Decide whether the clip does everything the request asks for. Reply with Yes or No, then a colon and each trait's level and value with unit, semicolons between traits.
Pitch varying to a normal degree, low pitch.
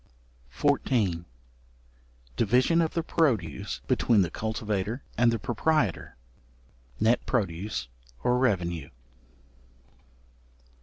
Yes: average, 5.0 semitones; low, 110 Hz